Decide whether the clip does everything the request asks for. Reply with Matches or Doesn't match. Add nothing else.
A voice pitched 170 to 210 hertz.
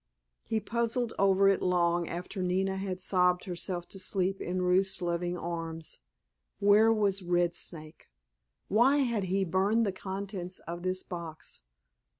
Matches